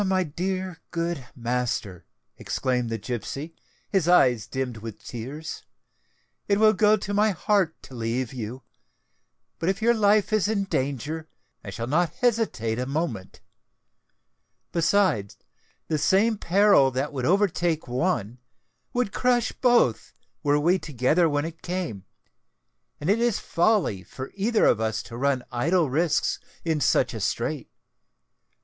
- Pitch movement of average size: No, wide, 7.6 semitones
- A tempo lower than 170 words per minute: Yes, average, 140 wpm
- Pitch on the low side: No, medium, 160 Hz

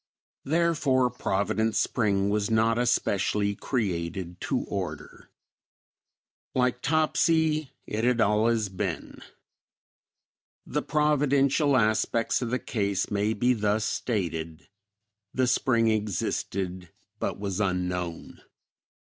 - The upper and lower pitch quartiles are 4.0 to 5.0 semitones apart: Yes, average, 4.4 semitones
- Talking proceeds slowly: Yes, slow, 100 wpm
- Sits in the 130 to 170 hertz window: No, low, 110 Hz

